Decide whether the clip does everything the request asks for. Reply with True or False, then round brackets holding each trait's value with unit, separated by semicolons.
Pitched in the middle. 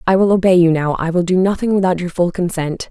True (180 Hz)